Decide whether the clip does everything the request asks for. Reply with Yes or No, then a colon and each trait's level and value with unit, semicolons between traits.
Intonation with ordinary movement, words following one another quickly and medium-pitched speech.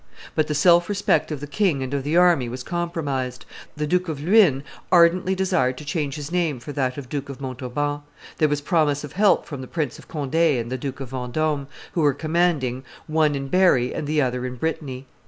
Yes: average, 4.0 semitones; fast, 215 wpm; medium, 145 Hz